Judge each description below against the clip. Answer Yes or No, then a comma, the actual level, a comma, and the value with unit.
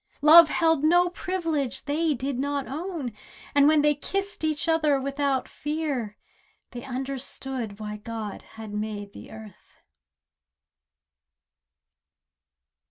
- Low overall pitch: No, very high, 280 Hz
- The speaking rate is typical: No, slow, 110 wpm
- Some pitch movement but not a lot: Yes, average, 4.7 semitones